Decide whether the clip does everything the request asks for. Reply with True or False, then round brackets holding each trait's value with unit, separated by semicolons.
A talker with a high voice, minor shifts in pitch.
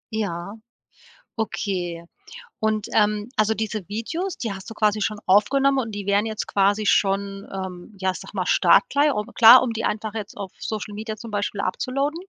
True (210 Hz; 2.1 semitones)